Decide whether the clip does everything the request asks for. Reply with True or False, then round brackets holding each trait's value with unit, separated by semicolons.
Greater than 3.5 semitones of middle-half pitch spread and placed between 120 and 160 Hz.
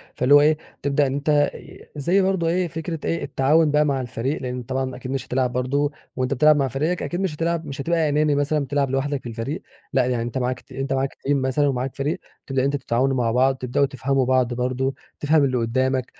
False (2.6 semitones; 135 Hz)